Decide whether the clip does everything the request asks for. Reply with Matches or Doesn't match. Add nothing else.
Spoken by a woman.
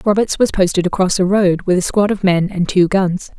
Matches